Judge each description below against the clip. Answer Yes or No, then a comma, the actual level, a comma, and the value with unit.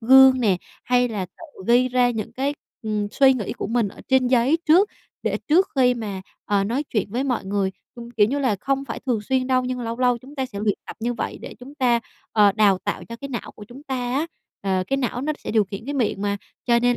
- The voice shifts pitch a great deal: No, average, 3.7 semitones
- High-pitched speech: Yes, high, 245 Hz